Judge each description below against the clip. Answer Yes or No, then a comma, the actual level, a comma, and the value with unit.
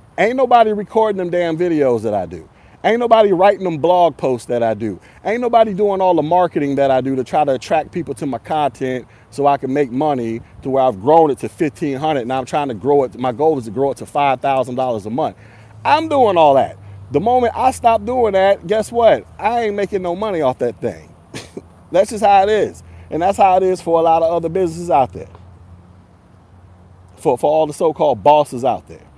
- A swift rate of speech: Yes, fast, 225 wpm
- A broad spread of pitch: Yes, wide, 7.6 semitones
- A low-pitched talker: No, medium, 150 Hz